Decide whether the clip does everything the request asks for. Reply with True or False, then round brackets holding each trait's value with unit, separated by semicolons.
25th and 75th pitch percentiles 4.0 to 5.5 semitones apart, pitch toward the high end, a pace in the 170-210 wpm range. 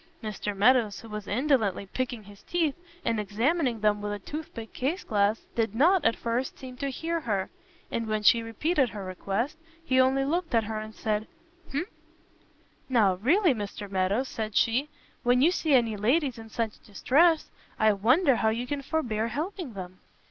True (4.7 semitones; 230 Hz; 180 wpm)